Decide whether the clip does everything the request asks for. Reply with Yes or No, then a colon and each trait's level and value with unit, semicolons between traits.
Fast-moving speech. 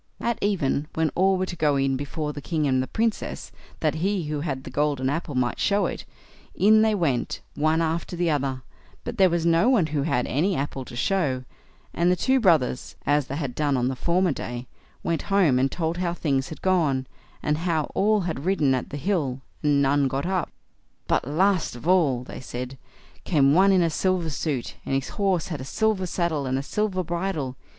Yes: fast, 210 wpm